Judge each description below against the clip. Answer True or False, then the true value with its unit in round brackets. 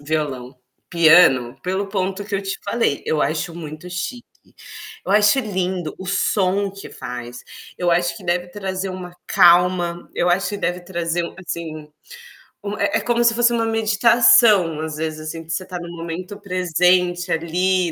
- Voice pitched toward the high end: False (180 Hz)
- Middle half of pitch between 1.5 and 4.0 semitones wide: True (3.1 semitones)